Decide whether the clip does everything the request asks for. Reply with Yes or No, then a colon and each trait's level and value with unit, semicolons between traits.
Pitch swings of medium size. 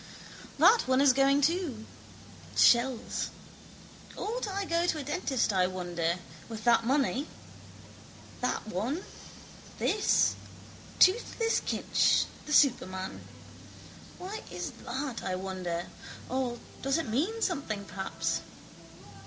No: wide, 8.5 semitones